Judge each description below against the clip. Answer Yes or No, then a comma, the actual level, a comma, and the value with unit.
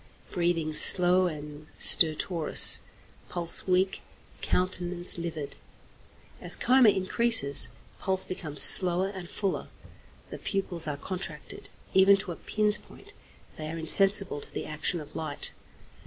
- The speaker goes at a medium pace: No, slow, 125 wpm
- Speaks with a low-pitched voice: No, medium, 175 Hz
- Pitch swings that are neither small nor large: Yes, average, 3.5 semitones